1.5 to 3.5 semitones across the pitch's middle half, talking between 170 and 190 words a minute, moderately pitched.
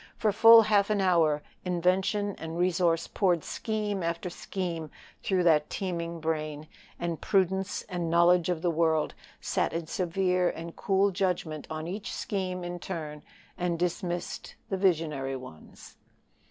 No: narrow, 2.6 semitones; average, 140 wpm; medium, 175 Hz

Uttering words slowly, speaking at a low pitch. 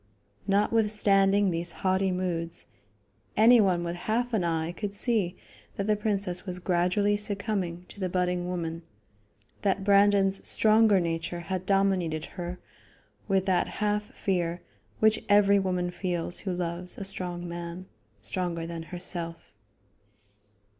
No: slow, 125 wpm; medium, 185 Hz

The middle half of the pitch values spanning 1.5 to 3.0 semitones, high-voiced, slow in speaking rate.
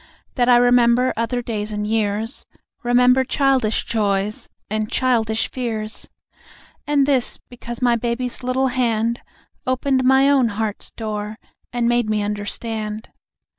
Yes: average, 2.7 semitones; high, 235 Hz; slow, 130 wpm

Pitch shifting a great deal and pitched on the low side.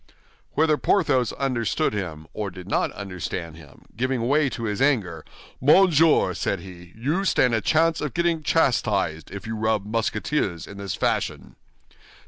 Yes: wide, 7.3 semitones; low, 110 Hz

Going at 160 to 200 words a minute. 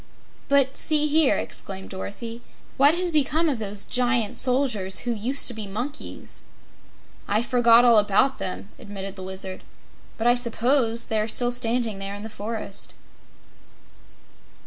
No: average, 145 wpm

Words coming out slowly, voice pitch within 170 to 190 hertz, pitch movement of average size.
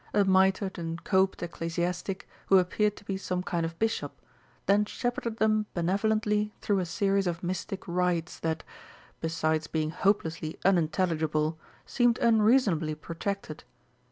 Yes: slow, 130 wpm; medium, 185 Hz; average, 3.7 semitones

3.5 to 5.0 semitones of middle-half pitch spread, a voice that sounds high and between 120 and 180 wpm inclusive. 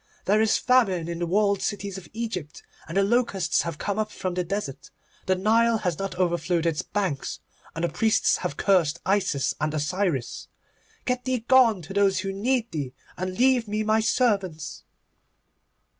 Yes: average, 4.1 semitones; high, 195 Hz; average, 175 wpm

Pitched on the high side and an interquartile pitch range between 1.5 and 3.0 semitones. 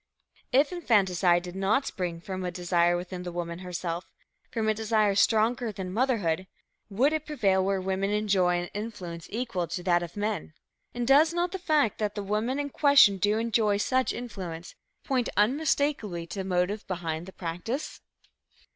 No: high, 200 Hz; average, 5.0 semitones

